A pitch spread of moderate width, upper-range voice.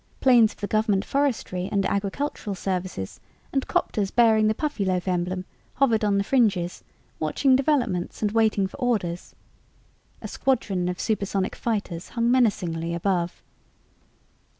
Yes: average, 4.3 semitones; high, 205 Hz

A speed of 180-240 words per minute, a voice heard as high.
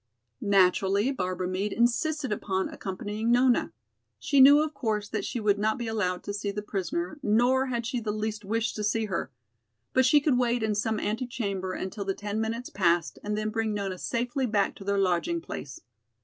Yes: average, 190 wpm; high, 215 Hz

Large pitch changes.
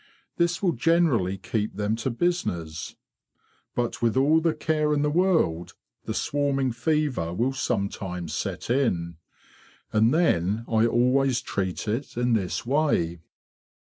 Yes: wide, 7.1 semitones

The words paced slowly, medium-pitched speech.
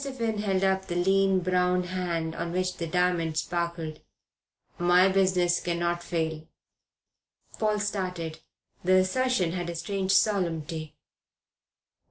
Yes: slow, 120 wpm; medium, 180 Hz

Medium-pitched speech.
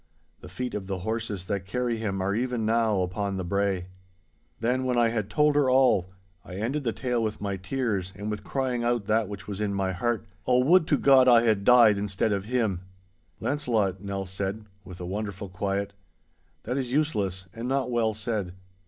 No: low, 110 Hz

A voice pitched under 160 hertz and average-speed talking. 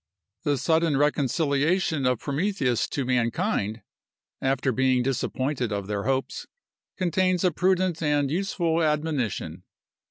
No: medium, 140 Hz; slow, 115 wpm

